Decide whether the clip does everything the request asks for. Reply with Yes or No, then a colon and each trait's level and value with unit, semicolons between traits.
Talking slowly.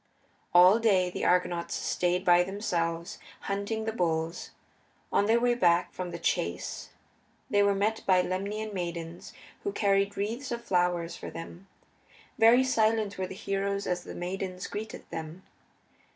No: average, 150 wpm